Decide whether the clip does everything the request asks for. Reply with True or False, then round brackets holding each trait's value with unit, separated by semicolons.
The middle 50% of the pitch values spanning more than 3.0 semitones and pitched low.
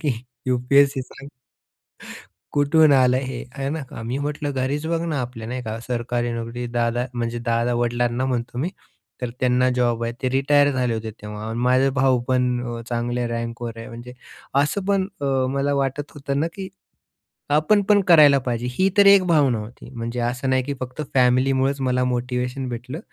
False (2.7 semitones; 125 Hz)